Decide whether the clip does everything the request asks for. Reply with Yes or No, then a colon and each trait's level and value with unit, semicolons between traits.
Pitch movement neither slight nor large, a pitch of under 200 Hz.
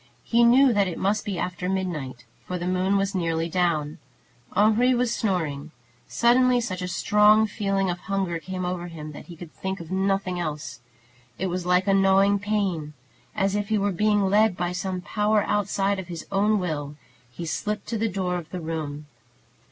Yes: average, 3.0 semitones; high, 190 Hz